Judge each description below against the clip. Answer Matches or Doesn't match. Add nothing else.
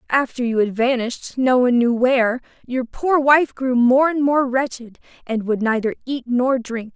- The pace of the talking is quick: Doesn't match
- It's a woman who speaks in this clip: Matches